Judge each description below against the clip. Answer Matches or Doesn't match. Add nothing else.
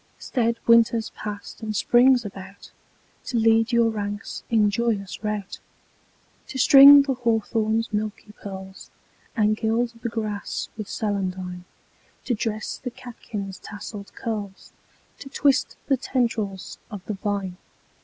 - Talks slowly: Matches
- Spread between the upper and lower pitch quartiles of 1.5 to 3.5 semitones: Matches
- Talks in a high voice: Matches